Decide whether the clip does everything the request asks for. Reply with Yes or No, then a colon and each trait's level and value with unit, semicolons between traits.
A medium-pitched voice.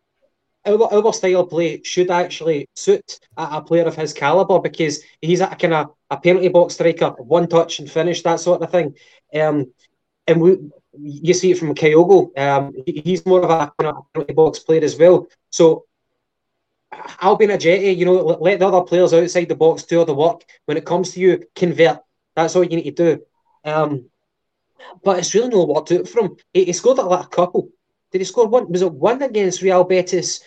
Yes: medium, 175 Hz